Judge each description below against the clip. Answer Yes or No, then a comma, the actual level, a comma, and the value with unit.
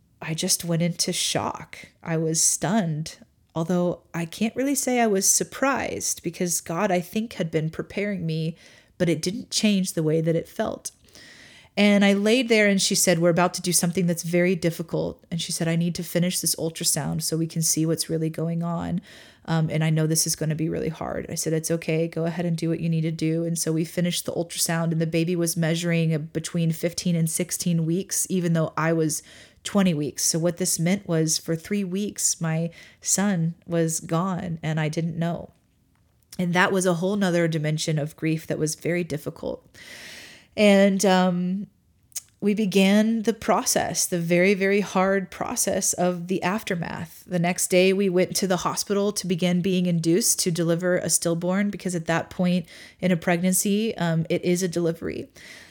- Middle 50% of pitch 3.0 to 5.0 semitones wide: No, narrow, 2.4 semitones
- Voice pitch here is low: No, medium, 175 Hz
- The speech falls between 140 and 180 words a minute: No, average, 195 wpm